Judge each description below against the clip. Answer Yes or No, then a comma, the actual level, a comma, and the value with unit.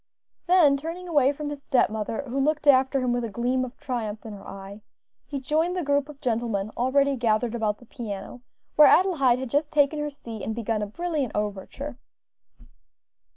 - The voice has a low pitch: No, very high, 260 Hz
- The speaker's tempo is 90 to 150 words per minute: No, average, 190 wpm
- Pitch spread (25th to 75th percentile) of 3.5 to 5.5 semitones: Yes, average, 4.6 semitones